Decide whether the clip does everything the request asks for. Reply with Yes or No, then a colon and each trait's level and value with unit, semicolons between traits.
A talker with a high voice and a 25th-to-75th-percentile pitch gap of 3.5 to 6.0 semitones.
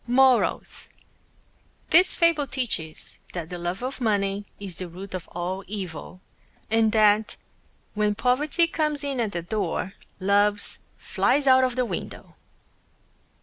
Yes: high, 210 Hz; wide, 5.5 semitones